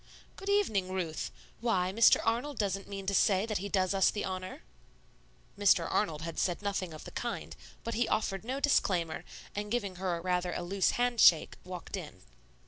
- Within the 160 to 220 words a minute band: Yes, average, 185 wpm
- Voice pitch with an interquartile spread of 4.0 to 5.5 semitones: No, average, 3.2 semitones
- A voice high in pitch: Yes, high, 195 Hz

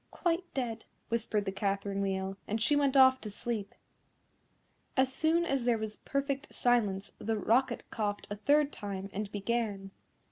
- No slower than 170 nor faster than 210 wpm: No, average, 155 wpm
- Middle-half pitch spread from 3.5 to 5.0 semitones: Yes, average, 4.7 semitones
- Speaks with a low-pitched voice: No, high, 225 Hz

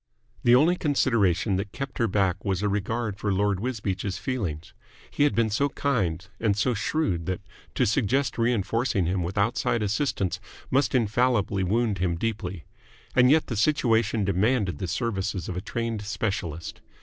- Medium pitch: No, low, 105 Hz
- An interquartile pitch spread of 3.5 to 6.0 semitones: Yes, average, 4.1 semitones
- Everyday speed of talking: Yes, average, 160 wpm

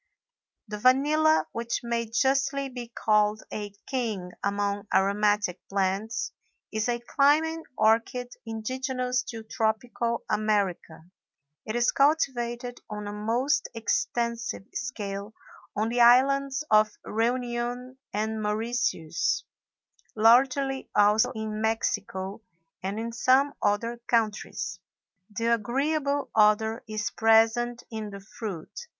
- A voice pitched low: No, high, 230 Hz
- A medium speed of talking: No, slow, 110 wpm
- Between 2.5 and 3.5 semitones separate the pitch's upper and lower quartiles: Yes, average, 2.9 semitones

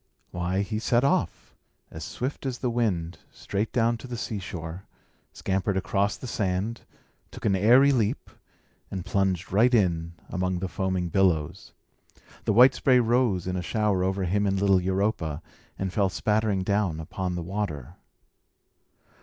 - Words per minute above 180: No, average, 155 wpm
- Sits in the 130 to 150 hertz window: No, very low, 95 Hz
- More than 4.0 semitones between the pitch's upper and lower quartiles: No, average, 3.2 semitones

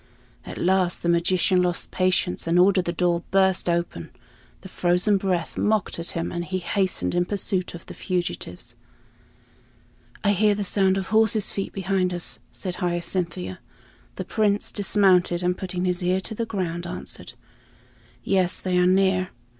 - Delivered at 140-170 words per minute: Yes, average, 160 wpm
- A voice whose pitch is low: No, medium, 185 Hz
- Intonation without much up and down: Yes, narrow, 1.8 semitones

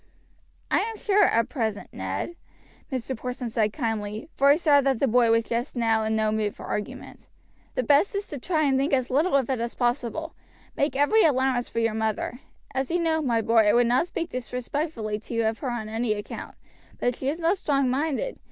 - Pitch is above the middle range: Yes, very high, 250 Hz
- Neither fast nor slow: No, fast, 215 wpm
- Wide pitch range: No, average, 4.3 semitones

